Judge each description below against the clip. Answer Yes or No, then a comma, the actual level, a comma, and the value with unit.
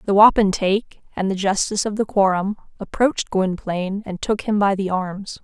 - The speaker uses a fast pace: No, average, 175 wpm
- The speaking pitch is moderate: No, high, 200 Hz